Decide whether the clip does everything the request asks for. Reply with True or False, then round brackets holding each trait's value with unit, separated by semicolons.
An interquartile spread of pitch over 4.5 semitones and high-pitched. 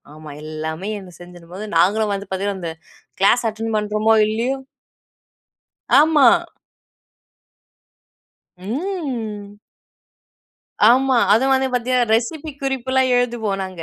True (5.0 semitones; 220 Hz)